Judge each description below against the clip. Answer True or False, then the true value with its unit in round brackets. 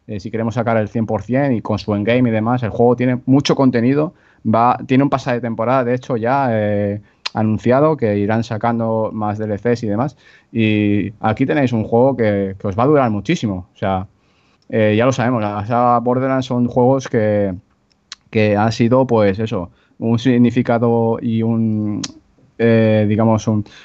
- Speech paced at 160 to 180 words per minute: True (175 wpm)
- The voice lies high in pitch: False (115 Hz)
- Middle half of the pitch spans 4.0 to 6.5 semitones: False (2.6 semitones)